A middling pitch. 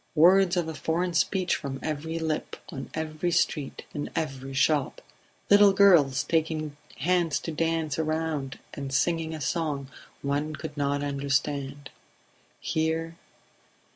Yes: medium, 155 Hz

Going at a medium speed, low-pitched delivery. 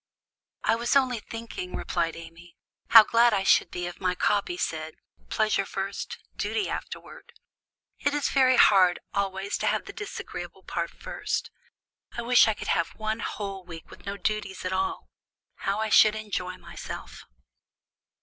No: average, 160 wpm; high, 200 Hz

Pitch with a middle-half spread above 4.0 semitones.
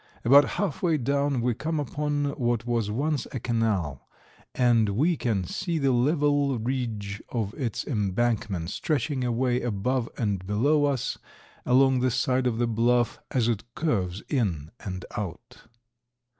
Yes: average, 4.5 semitones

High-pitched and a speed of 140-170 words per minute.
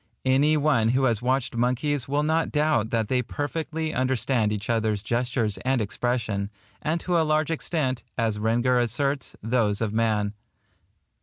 No: low, 125 Hz; average, 155 wpm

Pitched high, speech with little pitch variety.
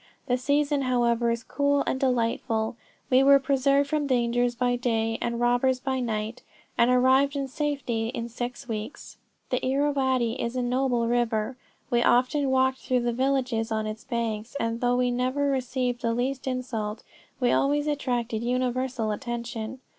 Yes: very high, 250 Hz; narrow, 2.1 semitones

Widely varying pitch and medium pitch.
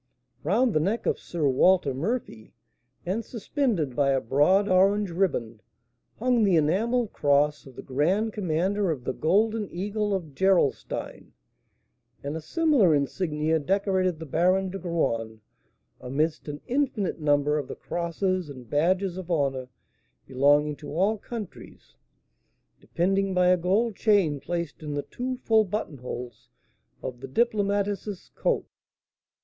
Yes: wide, 5.7 semitones; medium, 175 Hz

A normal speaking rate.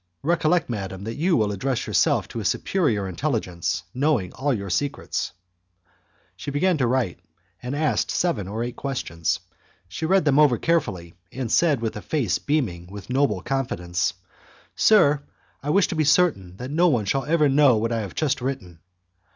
Yes: average, 175 wpm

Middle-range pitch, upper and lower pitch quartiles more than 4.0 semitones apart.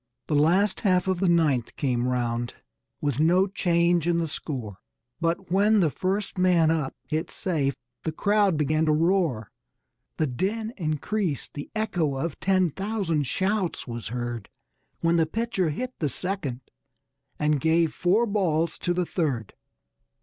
Yes: medium, 165 Hz; average, 4.5 semitones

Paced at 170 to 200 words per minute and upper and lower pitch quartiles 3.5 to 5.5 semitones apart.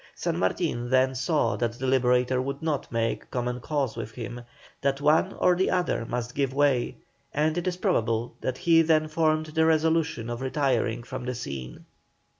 Yes: average, 180 wpm; average, 4.4 semitones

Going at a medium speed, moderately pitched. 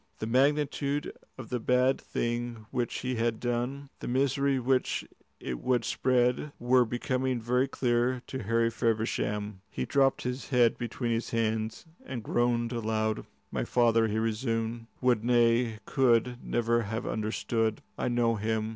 No: average, 145 wpm; low, 120 Hz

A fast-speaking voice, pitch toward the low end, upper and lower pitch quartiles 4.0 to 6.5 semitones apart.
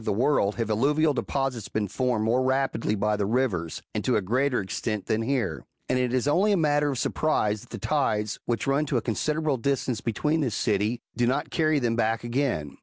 Yes: fast, 220 wpm; low, 125 Hz; average, 4.4 semitones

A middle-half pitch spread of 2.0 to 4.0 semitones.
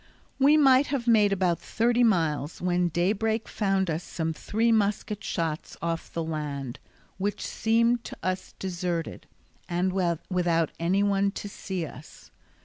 No: average, 4.5 semitones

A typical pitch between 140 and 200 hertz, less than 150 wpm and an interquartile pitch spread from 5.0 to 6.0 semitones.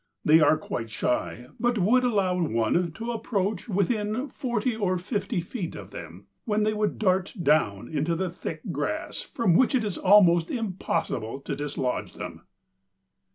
No: high, 190 Hz; average, 155 wpm; average, 5.3 semitones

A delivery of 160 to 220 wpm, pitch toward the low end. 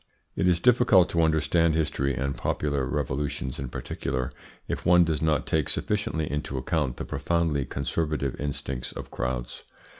No: average, 150 wpm; very low, 75 Hz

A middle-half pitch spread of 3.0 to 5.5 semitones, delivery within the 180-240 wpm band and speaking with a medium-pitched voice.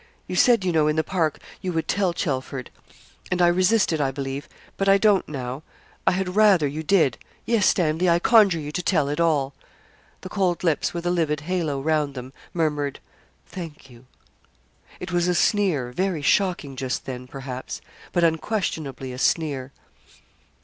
No: average, 4.6 semitones; average, 170 wpm; medium, 160 Hz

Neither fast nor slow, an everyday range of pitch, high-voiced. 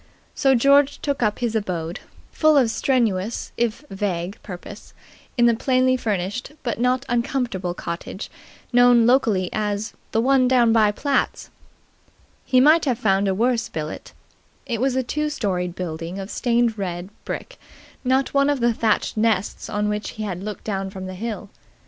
Yes: average, 165 wpm; average, 4.7 semitones; high, 225 Hz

